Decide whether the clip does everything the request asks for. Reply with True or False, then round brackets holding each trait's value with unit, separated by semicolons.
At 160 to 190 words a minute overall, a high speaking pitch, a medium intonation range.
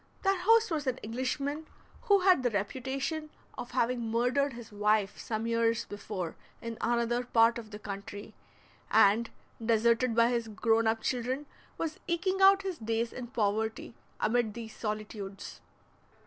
False (150 wpm; 235 Hz; 3.2 semitones)